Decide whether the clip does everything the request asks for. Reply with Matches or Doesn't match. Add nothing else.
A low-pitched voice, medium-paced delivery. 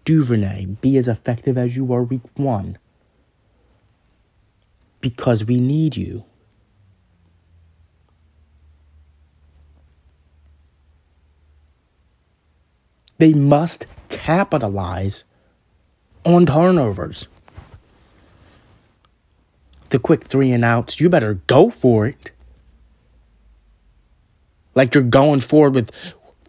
Doesn't match